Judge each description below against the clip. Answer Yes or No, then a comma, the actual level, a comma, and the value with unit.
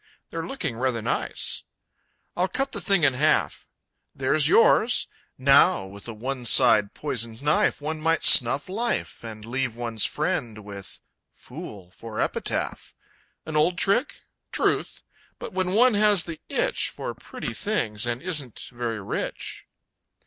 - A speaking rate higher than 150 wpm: No, average, 140 wpm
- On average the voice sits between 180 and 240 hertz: No, low, 135 Hz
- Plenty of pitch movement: Yes, wide, 7.2 semitones